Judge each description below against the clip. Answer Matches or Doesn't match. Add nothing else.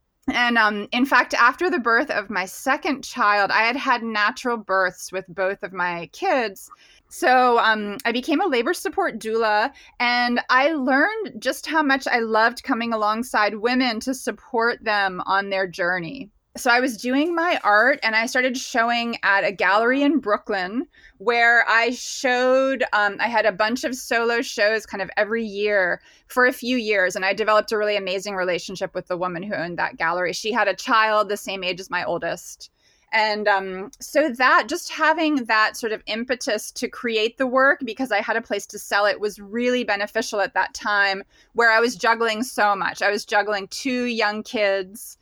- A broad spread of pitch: Doesn't match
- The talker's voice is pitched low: Doesn't match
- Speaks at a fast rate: Doesn't match